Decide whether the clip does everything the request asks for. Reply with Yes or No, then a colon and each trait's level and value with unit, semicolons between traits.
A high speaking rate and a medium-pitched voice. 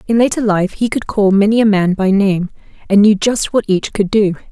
No: fast, 240 wpm; high, 205 Hz